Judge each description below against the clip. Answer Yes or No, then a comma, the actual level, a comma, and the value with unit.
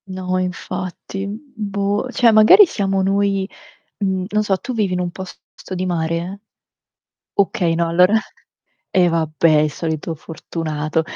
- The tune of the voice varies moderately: Yes, average, 3.1 semitones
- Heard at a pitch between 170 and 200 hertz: Yes, medium, 185 Hz